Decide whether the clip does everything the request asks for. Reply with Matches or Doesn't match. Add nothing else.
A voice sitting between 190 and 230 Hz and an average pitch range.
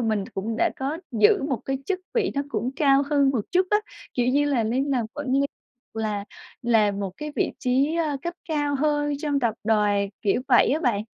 Doesn't match